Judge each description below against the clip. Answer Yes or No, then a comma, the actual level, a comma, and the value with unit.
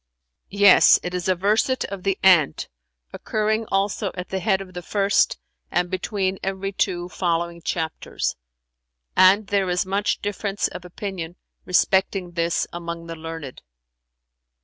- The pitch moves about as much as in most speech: No, narrow, 2.3 semitones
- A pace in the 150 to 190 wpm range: No, average, 140 wpm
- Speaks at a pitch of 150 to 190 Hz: Yes, medium, 185 Hz